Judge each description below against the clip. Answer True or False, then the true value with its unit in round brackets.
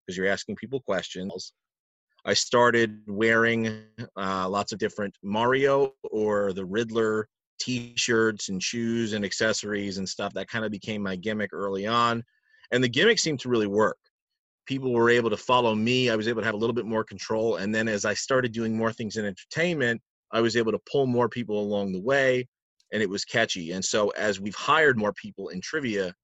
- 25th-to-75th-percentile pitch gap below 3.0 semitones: True (2.6 semitones)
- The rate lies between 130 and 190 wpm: False (200 wpm)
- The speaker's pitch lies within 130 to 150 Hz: False (110 Hz)